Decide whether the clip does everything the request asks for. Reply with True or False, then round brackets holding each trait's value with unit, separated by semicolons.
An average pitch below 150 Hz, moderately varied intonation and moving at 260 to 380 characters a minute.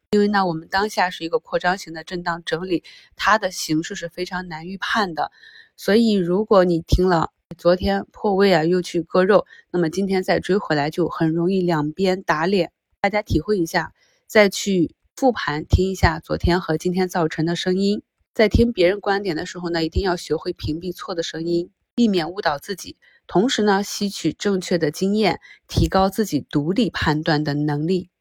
False (180 Hz; 3.2 semitones; 280 characters per minute)